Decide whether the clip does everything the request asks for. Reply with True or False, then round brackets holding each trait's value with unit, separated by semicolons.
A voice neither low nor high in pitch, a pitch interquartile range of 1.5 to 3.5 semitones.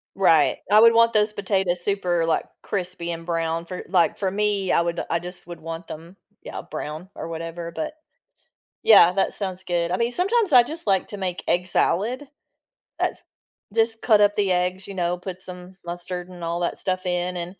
True (180 Hz; 2.9 semitones)